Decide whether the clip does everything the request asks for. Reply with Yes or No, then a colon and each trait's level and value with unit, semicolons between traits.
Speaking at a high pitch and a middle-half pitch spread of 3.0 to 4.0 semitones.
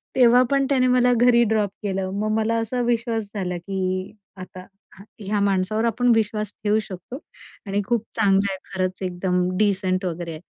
Yes: high, 205 Hz; average, 3.7 semitones